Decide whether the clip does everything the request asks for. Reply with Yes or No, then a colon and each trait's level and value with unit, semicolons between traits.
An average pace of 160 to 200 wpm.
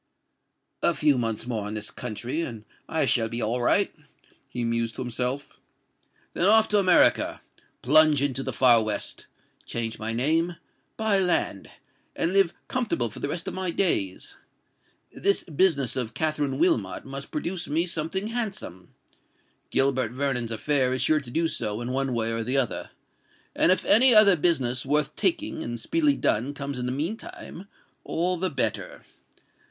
No: average, 150 wpm